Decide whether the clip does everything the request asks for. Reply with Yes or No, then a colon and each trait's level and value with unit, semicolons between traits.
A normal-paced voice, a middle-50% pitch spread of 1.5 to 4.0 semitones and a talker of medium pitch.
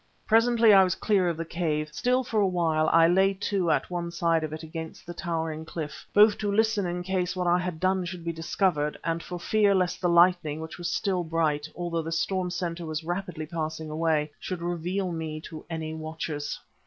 No: fast, 210 wpm; narrow, 2.6 semitones; medium, 170 Hz